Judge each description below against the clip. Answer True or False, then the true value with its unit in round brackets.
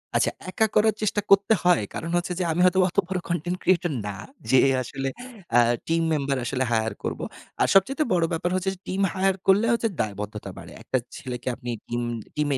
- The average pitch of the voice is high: False (175 Hz)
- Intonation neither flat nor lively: False (6.4 semitones)